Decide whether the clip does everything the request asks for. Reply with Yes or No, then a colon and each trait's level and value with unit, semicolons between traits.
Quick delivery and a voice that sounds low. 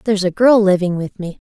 No: fast, 245 wpm; high, 195 Hz